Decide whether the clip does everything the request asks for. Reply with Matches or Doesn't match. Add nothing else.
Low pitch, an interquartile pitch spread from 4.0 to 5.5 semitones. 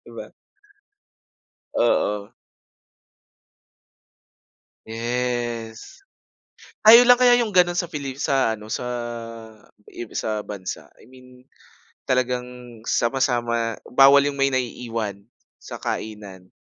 Doesn't match